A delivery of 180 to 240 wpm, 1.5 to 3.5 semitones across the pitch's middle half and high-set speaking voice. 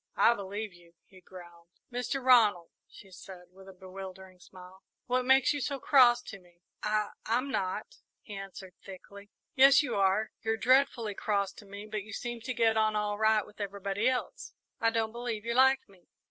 No: average, 190 wpm; average, 3.9 semitones; high, 210 Hz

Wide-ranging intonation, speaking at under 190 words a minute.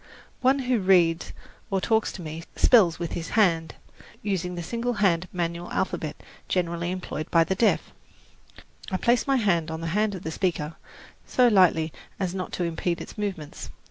No: average, 3.8 semitones; average, 175 wpm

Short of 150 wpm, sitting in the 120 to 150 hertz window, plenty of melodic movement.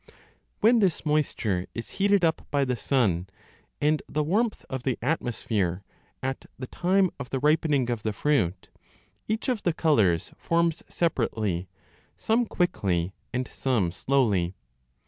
Yes: average, 140 wpm; low, 135 Hz; wide, 7.9 semitones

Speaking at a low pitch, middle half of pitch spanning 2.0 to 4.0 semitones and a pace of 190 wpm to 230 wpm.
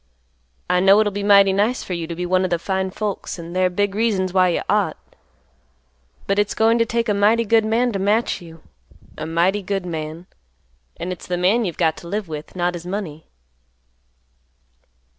No: high, 190 Hz; average, 3.0 semitones; average, 195 wpm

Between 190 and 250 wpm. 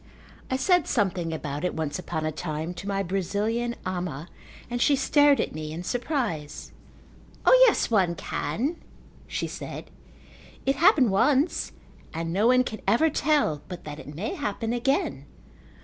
No: average, 155 wpm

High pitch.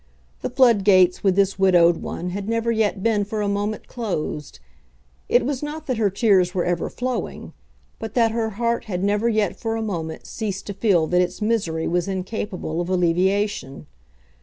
Yes: high, 200 Hz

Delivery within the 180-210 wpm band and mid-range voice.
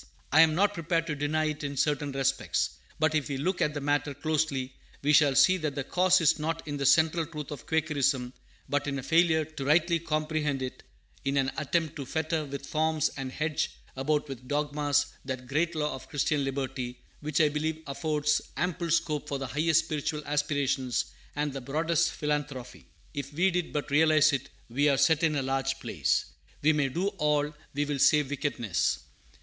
Yes: average, 190 wpm; medium, 150 Hz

